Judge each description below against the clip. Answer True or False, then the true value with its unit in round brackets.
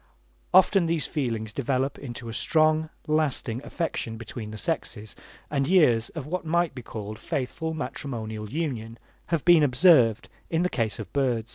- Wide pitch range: True (5.8 semitones)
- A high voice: False (135 Hz)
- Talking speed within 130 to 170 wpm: True (155 wpm)